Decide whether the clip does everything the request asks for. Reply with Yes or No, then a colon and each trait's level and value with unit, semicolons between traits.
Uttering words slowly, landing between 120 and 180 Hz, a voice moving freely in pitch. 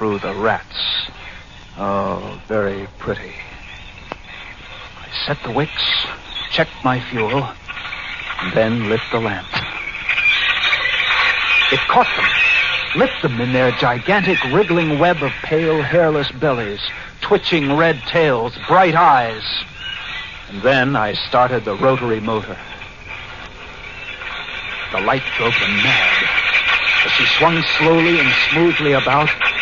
Yes: slow, 115 wpm; medium, 140 Hz; wide, 7.1 semitones